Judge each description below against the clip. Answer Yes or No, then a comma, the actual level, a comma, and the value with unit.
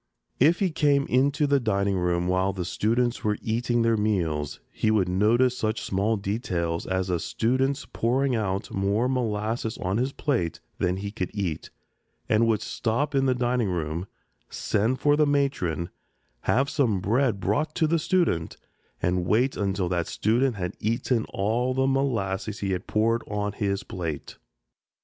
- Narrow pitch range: No, average, 5.2 semitones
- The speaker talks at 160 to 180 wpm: Yes, average, 165 wpm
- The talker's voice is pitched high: No, low, 110 Hz